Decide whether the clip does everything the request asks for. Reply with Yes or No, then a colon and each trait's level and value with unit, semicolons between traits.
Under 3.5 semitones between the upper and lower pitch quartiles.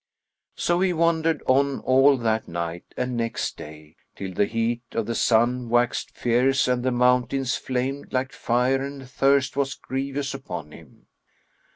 Yes: average, 2.8 semitones